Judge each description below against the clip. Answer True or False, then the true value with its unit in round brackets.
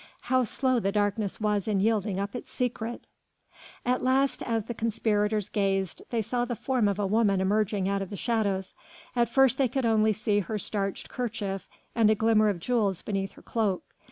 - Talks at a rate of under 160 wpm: False (190 wpm)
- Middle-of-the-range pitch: False (215 Hz)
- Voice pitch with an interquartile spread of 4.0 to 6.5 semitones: False (2.9 semitones)